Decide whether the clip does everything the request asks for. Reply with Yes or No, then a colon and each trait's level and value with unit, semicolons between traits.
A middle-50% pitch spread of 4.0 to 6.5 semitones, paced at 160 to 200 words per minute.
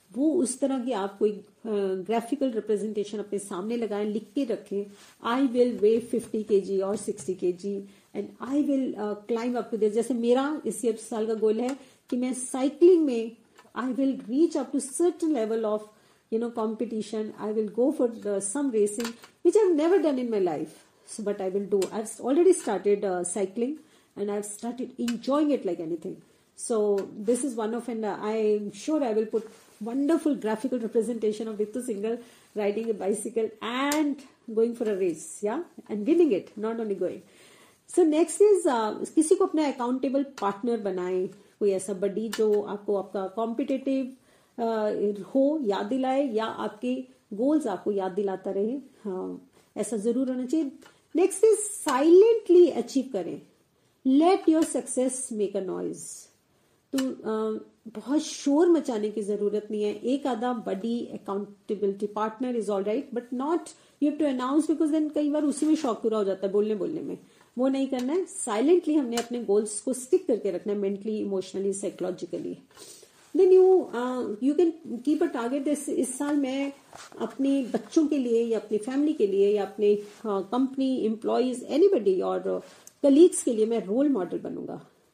Yes: average, 5.0 semitones; average, 170 wpm